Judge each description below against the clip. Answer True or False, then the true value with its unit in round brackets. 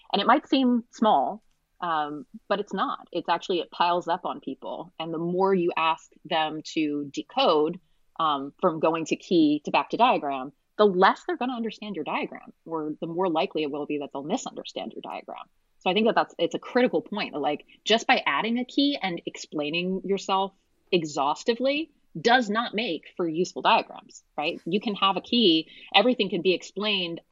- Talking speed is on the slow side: False (195 wpm)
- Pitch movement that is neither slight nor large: False (6.4 semitones)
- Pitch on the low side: False (190 Hz)